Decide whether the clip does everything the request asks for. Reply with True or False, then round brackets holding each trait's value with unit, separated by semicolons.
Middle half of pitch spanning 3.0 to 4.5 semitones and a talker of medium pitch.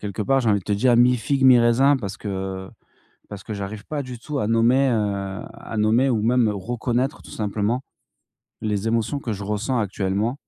False (3.6 semitones; 110 Hz)